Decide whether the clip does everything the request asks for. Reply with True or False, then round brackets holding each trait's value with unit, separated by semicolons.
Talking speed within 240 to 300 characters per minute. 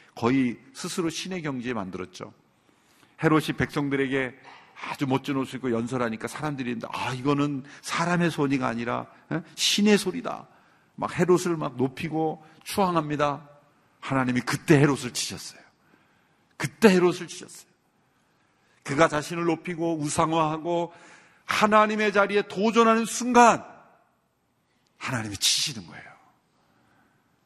True (285 characters per minute)